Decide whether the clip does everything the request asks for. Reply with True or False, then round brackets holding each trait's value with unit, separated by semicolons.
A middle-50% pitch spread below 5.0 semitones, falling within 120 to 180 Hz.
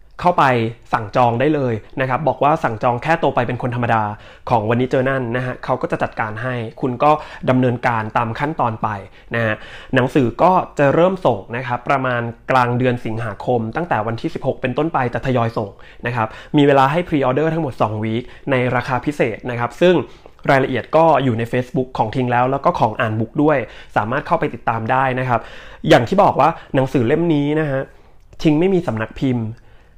True (3.8 semitones; 125 Hz)